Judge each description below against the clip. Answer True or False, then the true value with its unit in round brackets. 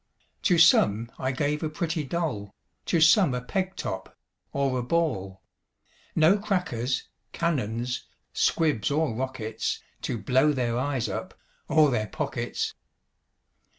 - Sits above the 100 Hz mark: True (135 Hz)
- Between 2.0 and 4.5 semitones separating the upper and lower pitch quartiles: False (5.5 semitones)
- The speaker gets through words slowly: True (125 wpm)